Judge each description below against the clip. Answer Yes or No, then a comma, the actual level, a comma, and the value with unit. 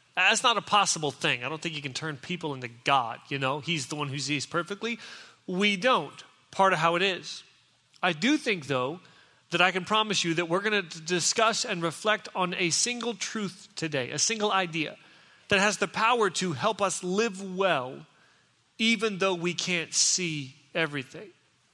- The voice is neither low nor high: Yes, medium, 180 Hz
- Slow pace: No, average, 190 wpm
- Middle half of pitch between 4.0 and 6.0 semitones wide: Yes, average, 4.5 semitones